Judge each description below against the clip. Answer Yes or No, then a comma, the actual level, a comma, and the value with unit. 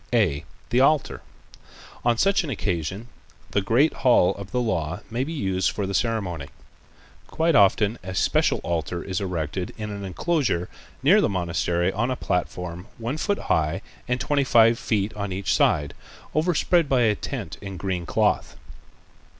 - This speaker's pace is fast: No, average, 160 wpm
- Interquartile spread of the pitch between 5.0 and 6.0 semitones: Yes, wide, 5.5 semitones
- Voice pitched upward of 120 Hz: No, low, 100 Hz